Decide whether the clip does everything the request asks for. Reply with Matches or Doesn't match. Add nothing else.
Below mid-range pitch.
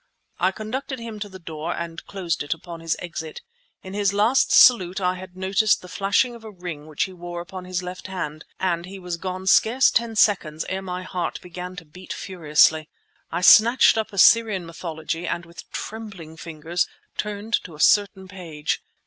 Doesn't match